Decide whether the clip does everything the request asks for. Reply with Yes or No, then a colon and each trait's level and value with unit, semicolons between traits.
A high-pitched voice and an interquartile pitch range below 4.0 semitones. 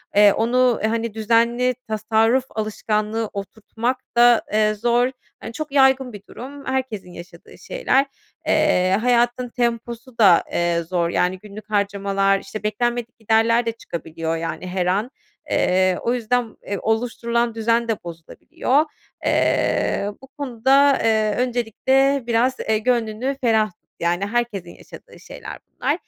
Yes: high, 225 Hz; average, 3.3 semitones